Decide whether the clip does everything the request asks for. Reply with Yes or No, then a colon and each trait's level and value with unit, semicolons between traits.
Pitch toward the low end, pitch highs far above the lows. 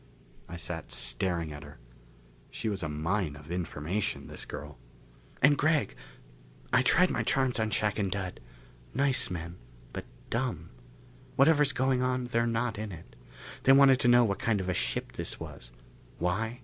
Yes: low, 105 Hz; wide, 6.9 semitones